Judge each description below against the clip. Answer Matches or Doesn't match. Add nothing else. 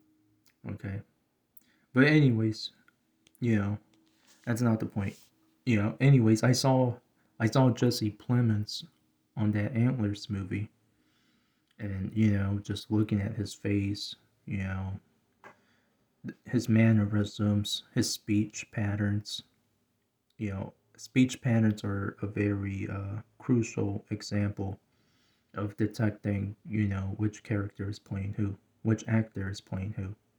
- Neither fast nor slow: Doesn't match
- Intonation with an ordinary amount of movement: Doesn't match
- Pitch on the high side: Doesn't match